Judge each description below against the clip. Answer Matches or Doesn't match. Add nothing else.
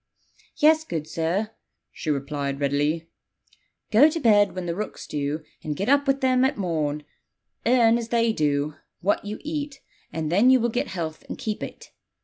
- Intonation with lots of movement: Matches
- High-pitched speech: Matches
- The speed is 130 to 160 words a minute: Doesn't match